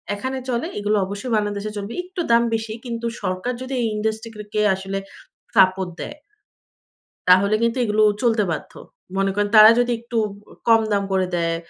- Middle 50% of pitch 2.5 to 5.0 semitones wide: Yes, average, 2.9 semitones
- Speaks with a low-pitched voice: No, high, 215 Hz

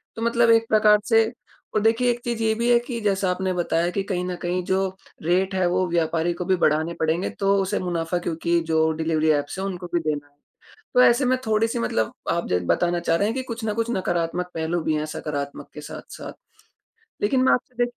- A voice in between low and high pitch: Yes, medium, 180 Hz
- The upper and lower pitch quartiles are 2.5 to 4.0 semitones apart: No, average, 5.3 semitones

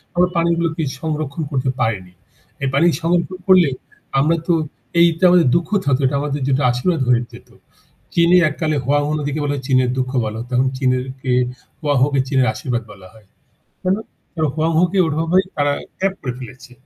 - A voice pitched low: No, medium, 145 Hz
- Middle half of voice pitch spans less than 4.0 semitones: No, average, 4.4 semitones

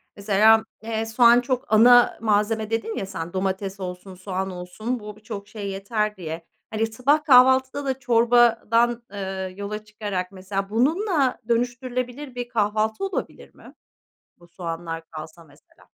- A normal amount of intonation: Yes, average, 4.0 semitones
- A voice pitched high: Yes, high, 215 Hz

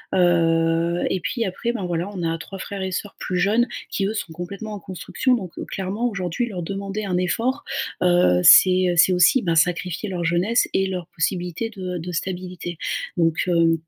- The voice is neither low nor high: Yes, medium, 180 Hz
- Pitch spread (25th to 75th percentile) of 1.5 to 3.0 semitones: Yes, narrow, 2.5 semitones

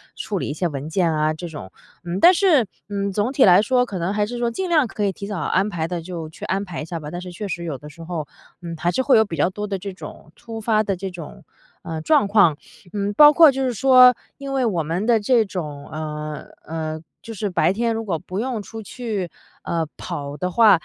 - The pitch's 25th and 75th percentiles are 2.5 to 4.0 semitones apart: No, average, 5.3 semitones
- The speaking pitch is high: Yes, high, 195 Hz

